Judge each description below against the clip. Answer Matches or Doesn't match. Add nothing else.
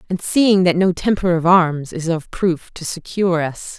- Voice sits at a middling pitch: Matches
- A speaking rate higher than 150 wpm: Matches